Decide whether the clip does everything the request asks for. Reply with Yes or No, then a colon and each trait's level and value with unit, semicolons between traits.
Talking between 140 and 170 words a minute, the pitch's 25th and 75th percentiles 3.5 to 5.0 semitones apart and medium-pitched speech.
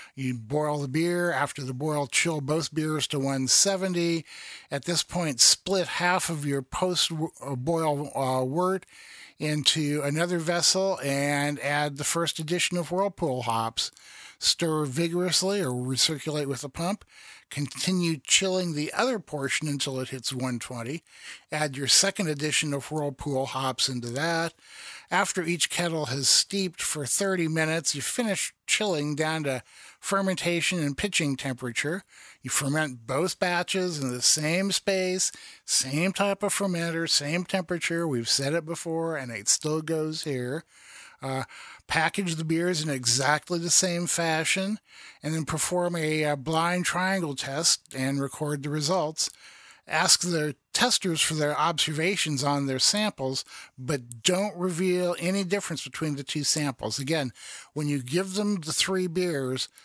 Yes: average, 145 wpm; average, 3.9 semitones; medium, 155 Hz